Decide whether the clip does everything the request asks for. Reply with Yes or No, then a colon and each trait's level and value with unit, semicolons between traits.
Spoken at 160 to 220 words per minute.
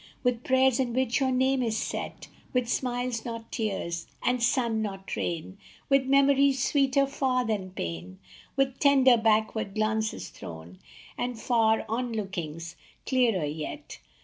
No: average, 140 wpm